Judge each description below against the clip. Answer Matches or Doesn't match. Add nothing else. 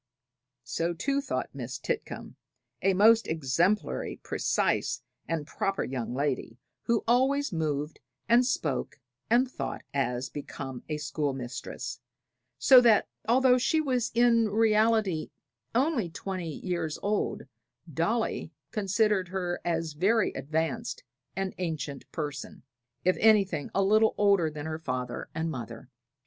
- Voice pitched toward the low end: Doesn't match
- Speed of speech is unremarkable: Doesn't match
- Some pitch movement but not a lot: Doesn't match